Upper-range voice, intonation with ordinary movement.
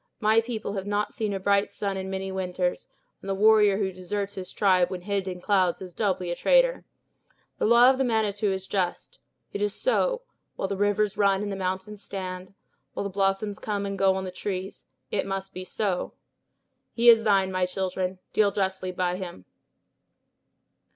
No: high, 195 Hz; narrow, 1.8 semitones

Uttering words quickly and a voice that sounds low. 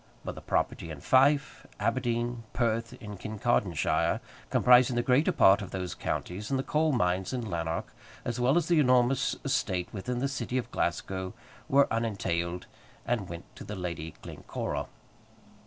No: average, 160 wpm; low, 115 Hz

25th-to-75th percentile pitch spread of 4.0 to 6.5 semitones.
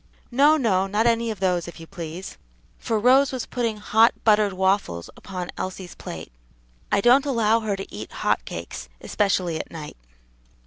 Yes: average, 4.3 semitones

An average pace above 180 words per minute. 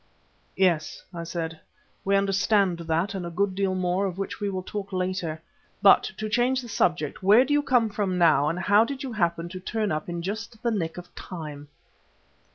Yes: average, 200 wpm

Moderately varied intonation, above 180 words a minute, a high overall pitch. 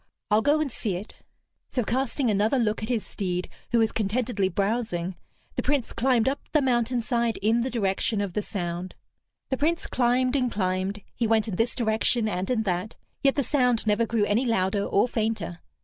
Yes: average, 3.6 semitones; average, 190 wpm; high, 225 Hz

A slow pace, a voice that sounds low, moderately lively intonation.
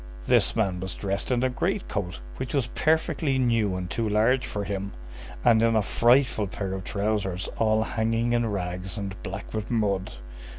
No: average, 180 wpm; low, 110 Hz; average, 3.6 semitones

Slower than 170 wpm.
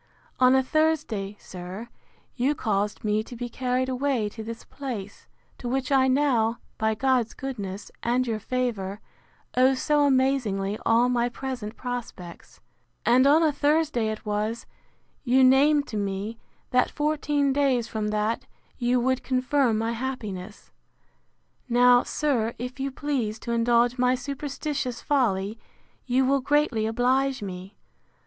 Yes: average, 140 wpm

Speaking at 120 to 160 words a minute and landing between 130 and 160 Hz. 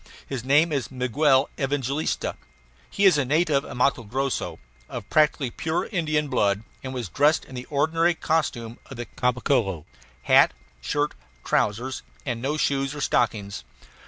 Yes: average, 150 wpm; low, 135 Hz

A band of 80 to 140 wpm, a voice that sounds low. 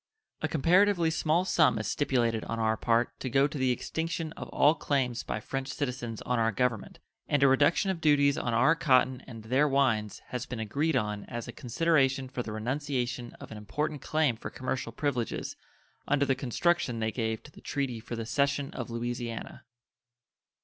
No: average, 185 wpm; low, 130 Hz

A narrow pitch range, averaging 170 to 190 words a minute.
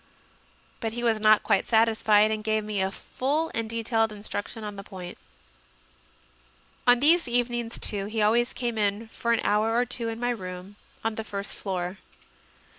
Yes: narrow, 2.3 semitones; average, 175 wpm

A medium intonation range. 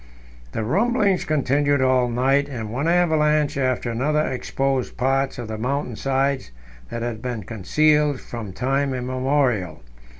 Yes: average, 3.0 semitones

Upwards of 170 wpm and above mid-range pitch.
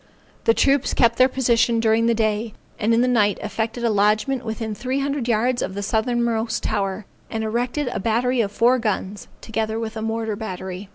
Yes: average, 190 wpm; high, 225 Hz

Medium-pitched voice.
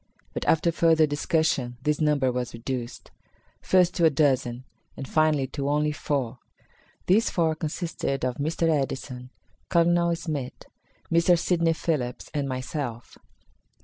Yes: medium, 150 Hz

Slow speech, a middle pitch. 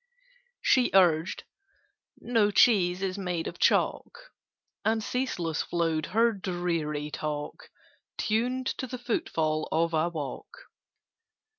Yes: slow, 110 wpm; medium, 180 Hz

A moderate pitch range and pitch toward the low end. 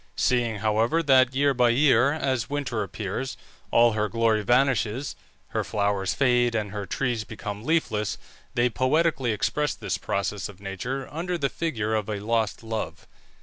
Yes: average, 4.0 semitones; low, 115 Hz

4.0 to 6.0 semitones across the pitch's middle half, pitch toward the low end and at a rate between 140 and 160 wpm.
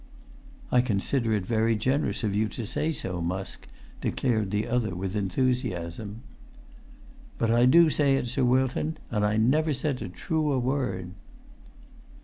Yes: average, 4.4 semitones; low, 115 Hz; average, 145 wpm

